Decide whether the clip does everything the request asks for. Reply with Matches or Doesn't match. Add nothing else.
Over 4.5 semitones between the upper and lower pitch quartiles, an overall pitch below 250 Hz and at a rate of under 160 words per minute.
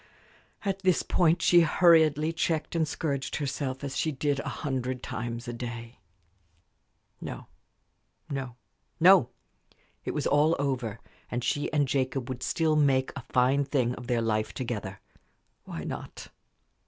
Doesn't match